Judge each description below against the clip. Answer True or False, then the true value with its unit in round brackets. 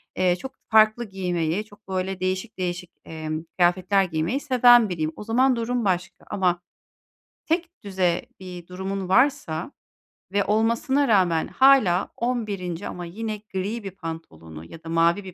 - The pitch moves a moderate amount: True (4.2 semitones)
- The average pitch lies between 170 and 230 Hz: True (190 Hz)